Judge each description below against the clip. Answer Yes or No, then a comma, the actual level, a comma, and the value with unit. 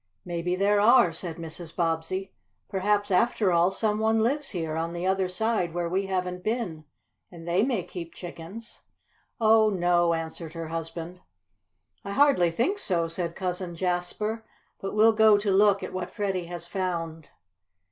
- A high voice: No, medium, 180 Hz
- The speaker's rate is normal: Yes, average, 160 wpm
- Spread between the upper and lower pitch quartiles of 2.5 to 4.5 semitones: Yes, average, 3.6 semitones